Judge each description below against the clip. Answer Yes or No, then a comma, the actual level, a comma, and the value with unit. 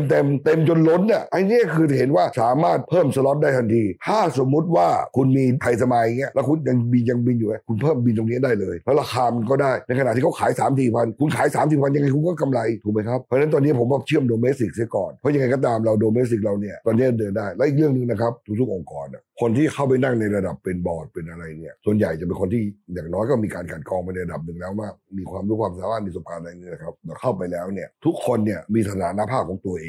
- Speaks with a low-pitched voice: Yes, low, 120 Hz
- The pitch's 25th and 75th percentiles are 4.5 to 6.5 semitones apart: Yes, average, 5.0 semitones